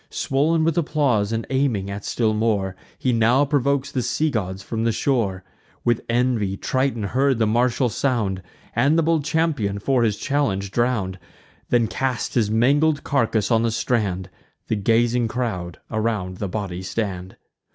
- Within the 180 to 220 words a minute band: No, average, 160 wpm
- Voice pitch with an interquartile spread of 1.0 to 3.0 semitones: No, average, 4.7 semitones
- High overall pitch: No, low, 115 Hz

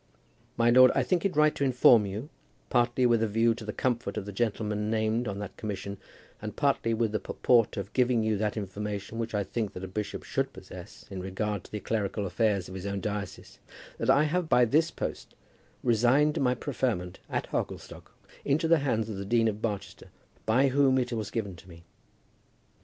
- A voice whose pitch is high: No, low, 110 Hz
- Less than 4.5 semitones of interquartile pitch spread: Yes, average, 3.5 semitones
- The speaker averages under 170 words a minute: No, average, 200 wpm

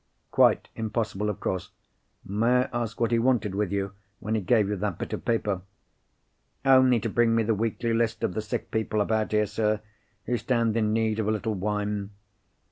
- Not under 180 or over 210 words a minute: Yes, average, 200 wpm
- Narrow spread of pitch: Yes, narrow, 1.8 semitones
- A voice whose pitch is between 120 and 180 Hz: No, low, 110 Hz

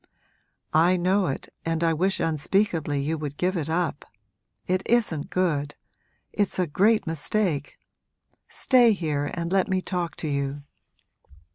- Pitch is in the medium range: Yes, medium, 170 Hz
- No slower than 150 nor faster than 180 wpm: No, average, 140 wpm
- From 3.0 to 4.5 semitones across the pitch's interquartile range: Yes, average, 4.1 semitones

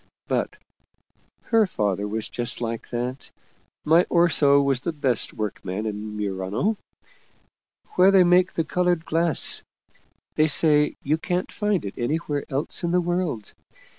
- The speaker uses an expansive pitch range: Yes, wide, 7.5 semitones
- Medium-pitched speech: Yes, medium, 150 Hz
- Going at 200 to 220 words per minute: No, slow, 135 wpm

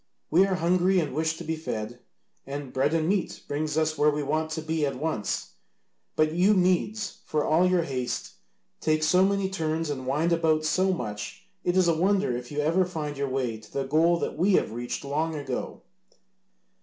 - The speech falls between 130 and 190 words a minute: No, average, 200 wpm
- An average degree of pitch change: Yes, average, 3.8 semitones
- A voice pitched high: No, medium, 155 Hz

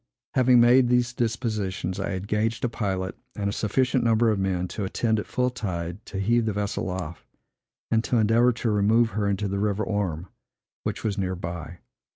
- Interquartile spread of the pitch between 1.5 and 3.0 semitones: No, average, 3.5 semitones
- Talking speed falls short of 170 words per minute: No, average, 190 wpm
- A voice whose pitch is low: Yes, low, 105 Hz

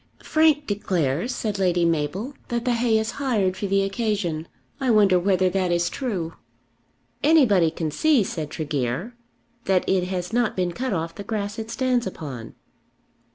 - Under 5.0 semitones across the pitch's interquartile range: No, average, 5.3 semitones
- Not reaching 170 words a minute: Yes, average, 160 wpm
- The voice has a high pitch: Yes, high, 195 Hz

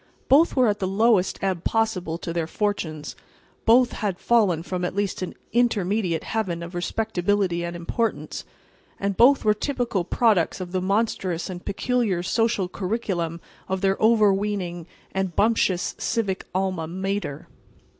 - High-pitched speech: Yes, high, 195 Hz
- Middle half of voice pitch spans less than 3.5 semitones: No, average, 3.9 semitones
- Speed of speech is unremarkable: Yes, average, 145 wpm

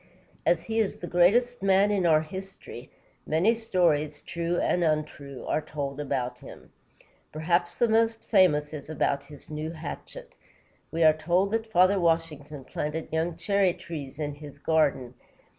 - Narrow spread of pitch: No, average, 4.0 semitones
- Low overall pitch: No, medium, 165 Hz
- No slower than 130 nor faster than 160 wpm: Yes, average, 155 wpm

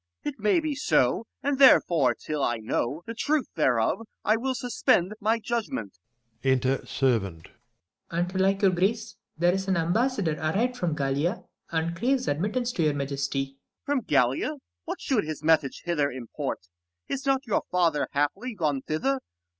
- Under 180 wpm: Yes, average, 170 wpm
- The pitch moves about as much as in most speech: No, wide, 8.5 semitones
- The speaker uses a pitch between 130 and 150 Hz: No, medium, 170 Hz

